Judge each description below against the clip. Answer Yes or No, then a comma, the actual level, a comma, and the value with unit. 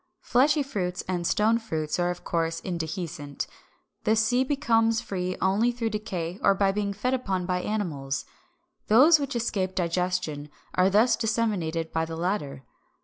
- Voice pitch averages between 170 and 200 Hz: Yes, high, 190 Hz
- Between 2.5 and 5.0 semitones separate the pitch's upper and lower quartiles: Yes, average, 4.7 semitones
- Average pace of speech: Yes, average, 150 wpm